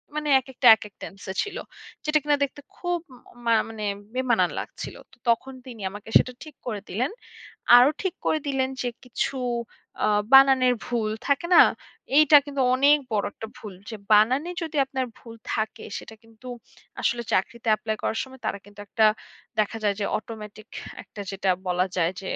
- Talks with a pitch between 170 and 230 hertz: No, high, 240 Hz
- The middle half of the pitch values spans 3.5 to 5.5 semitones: Yes, average, 4.0 semitones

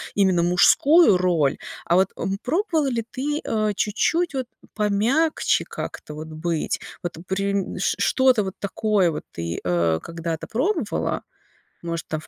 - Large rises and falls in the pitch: Yes, wide, 7.2 semitones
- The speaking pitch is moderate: No, high, 195 Hz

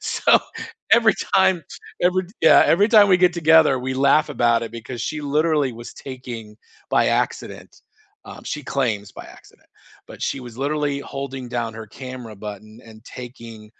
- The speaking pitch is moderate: No, low, 130 Hz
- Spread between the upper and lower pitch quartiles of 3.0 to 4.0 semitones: No, average, 4.8 semitones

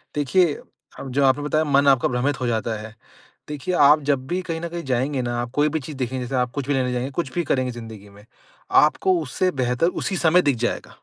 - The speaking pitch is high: No, low, 135 Hz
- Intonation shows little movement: No, average, 3.8 semitones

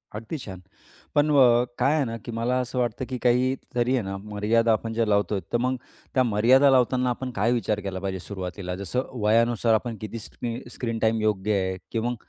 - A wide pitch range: No, average, 3.1 semitones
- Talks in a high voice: No, low, 115 Hz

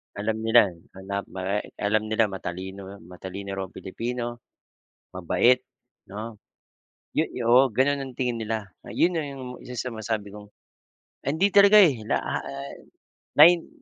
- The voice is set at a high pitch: No, low, 110 Hz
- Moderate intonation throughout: Yes, average, 4.4 semitones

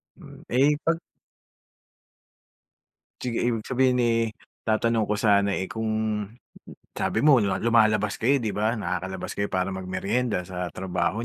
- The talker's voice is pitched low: Yes, low, 110 Hz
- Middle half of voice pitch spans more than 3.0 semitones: Yes, average, 3.8 semitones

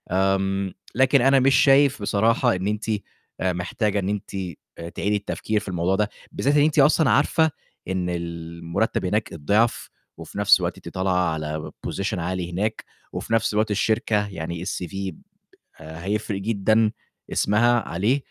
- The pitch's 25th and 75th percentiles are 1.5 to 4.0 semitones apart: Yes, average, 3.7 semitones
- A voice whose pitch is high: No, low, 100 Hz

